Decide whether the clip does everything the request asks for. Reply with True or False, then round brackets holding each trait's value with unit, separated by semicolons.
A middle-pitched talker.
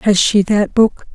False (205 Hz)